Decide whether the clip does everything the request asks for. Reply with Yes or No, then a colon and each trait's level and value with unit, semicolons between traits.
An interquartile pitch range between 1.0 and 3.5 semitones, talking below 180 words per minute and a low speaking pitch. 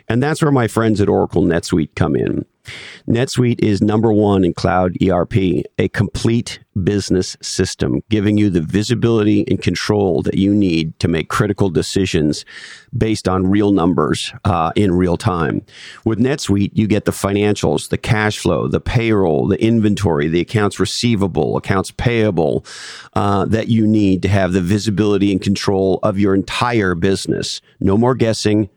Yes: average, 2.8 semitones; average, 160 wpm; low, 100 Hz